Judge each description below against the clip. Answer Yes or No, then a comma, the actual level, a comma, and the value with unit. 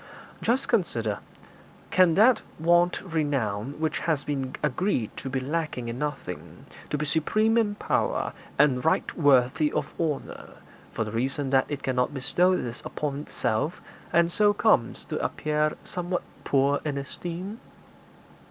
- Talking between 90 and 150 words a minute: Yes, average, 145 wpm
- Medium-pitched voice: Yes, medium, 150 Hz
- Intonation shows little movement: No, average, 4.6 semitones